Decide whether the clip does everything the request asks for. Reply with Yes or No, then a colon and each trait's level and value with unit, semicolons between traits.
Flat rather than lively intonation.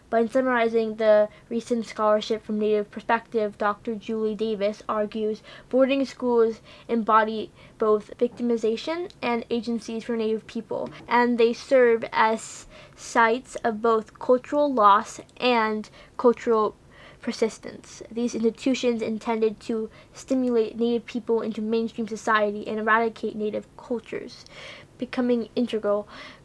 Yes: narrow, 1.7 semitones